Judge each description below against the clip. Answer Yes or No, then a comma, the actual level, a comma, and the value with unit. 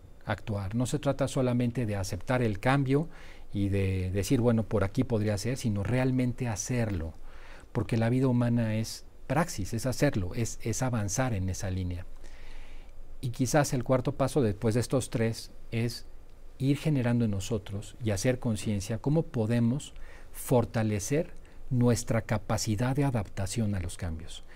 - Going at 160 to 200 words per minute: No, average, 150 wpm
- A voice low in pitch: Yes, low, 115 Hz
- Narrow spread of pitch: No, average, 4.2 semitones